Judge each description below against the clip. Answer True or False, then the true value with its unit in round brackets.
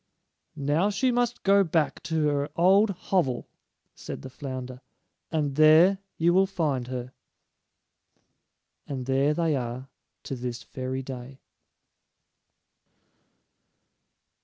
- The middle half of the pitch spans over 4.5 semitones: True (5.1 semitones)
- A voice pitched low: False (145 Hz)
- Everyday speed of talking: False (110 wpm)